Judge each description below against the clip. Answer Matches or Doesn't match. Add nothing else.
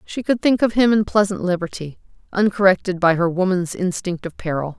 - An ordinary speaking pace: Matches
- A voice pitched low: Doesn't match